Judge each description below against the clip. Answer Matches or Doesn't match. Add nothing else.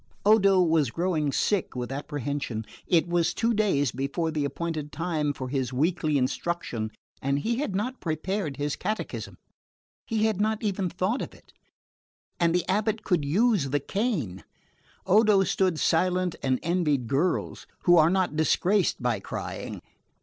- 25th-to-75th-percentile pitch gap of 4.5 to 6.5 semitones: Matches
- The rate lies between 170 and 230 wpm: Doesn't match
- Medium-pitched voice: Matches